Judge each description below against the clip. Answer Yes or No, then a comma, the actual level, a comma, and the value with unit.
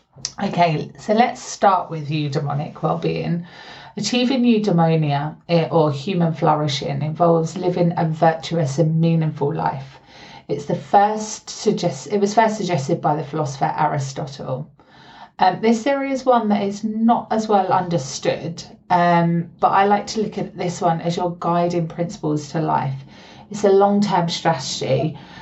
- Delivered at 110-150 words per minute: Yes, average, 145 wpm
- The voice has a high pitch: No, medium, 175 Hz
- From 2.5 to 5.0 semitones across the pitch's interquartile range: Yes, average, 4.1 semitones